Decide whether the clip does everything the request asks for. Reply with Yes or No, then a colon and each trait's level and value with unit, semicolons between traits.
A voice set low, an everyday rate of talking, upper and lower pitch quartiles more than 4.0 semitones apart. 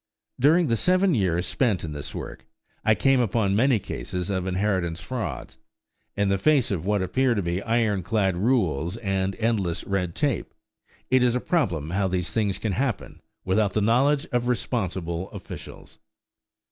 Yes: low, 100 Hz; average, 165 wpm; average, 5.0 semitones